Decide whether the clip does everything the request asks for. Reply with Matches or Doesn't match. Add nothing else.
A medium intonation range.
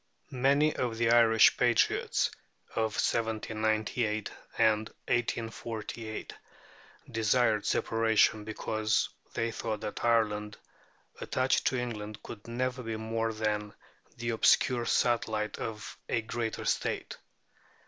Doesn't match